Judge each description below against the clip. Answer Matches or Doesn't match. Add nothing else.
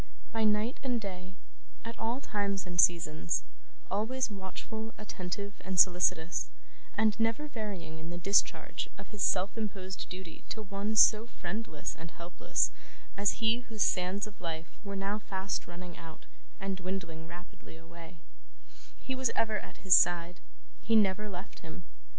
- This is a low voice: Doesn't match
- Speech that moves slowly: Doesn't match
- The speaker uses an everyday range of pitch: Matches